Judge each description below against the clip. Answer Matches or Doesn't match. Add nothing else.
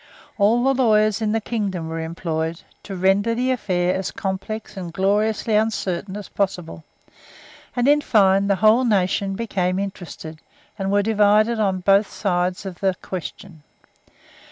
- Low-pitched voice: Doesn't match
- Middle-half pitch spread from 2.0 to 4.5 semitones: Matches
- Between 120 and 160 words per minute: Matches